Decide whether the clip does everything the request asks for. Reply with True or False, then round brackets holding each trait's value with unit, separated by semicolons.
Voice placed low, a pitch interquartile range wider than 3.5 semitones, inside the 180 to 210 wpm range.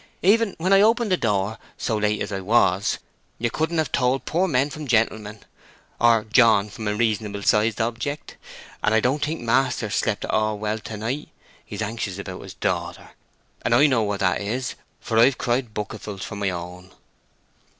True (110 Hz; 4.2 semitones; 185 wpm)